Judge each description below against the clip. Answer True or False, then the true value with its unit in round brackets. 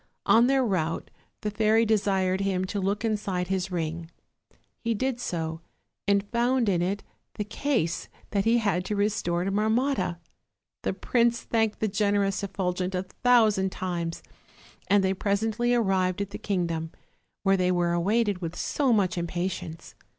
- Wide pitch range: False (3.3 semitones)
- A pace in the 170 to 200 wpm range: False (155 wpm)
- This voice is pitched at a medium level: False (195 Hz)